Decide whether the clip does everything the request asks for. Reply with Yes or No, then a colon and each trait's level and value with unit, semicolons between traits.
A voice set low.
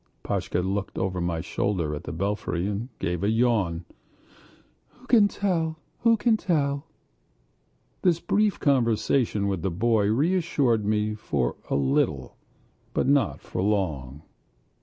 Yes: low, 105 Hz